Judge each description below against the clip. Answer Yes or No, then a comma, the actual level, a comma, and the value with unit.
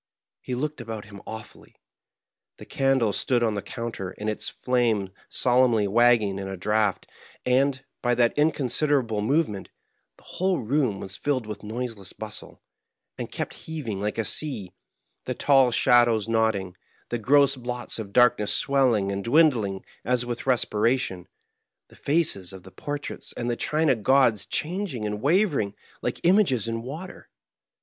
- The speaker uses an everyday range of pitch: Yes, average, 4.4 semitones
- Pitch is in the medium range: No, low, 120 Hz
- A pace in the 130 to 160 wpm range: Yes, average, 150 wpm